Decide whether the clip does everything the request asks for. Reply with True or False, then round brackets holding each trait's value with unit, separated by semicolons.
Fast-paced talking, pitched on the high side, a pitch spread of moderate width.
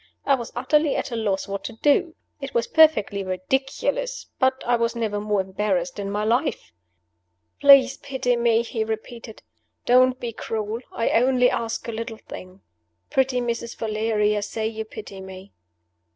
False (160 wpm; 230 Hz; 3.4 semitones)